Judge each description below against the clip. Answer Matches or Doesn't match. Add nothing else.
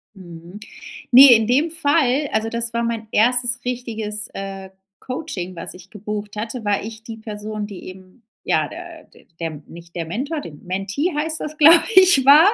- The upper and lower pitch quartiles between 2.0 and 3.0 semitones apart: Doesn't match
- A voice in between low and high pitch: Doesn't match